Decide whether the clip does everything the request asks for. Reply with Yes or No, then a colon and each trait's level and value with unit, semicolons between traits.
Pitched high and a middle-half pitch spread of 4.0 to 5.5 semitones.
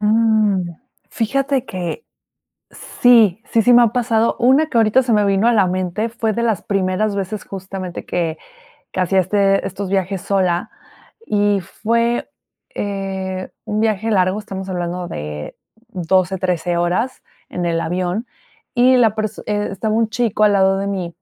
No: high, 200 Hz; average, 3.3 semitones